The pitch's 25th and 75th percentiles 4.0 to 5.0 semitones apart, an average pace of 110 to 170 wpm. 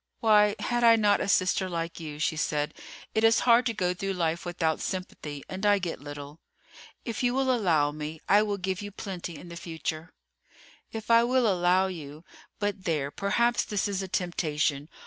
No: average, 4.6 semitones; average, 190 wpm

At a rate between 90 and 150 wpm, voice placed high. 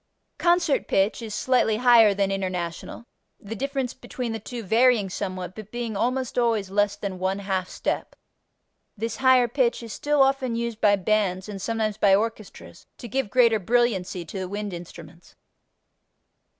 No: average, 160 wpm; high, 215 Hz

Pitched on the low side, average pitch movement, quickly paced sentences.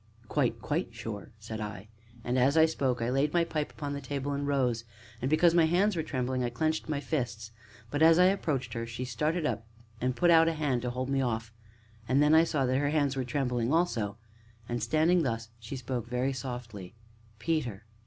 Yes: low, 130 Hz; average, 4.6 semitones; fast, 210 wpm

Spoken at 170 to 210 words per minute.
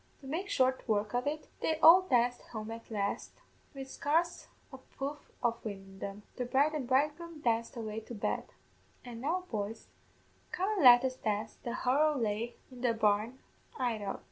Yes: average, 180 wpm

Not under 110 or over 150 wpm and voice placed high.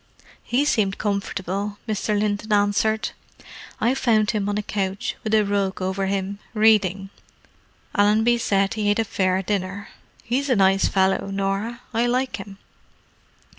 Yes: average, 145 wpm; high, 205 Hz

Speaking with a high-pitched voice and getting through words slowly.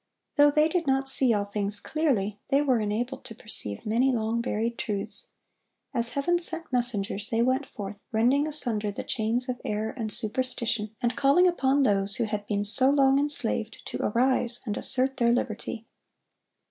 No: high, 235 Hz; average, 170 wpm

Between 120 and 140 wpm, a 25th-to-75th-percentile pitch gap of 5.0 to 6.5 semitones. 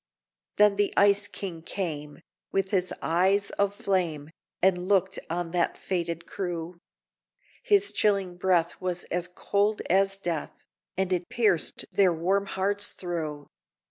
No: slow, 135 wpm; narrow, 2.6 semitones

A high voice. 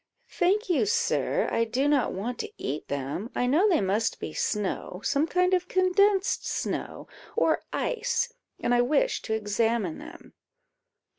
Yes: very high, 285 Hz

